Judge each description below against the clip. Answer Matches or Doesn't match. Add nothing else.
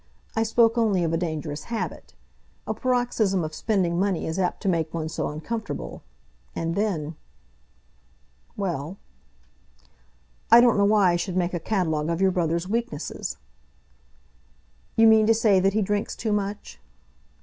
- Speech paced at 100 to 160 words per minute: Matches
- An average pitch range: Matches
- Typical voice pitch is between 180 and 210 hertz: Matches